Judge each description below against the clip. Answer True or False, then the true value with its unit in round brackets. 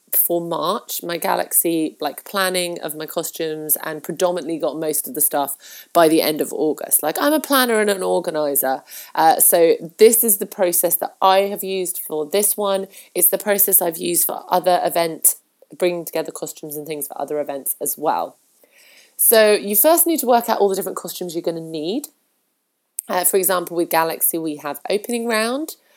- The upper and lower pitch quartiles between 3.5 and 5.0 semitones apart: True (4.1 semitones)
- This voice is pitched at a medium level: True (180 Hz)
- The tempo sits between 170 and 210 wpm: True (190 wpm)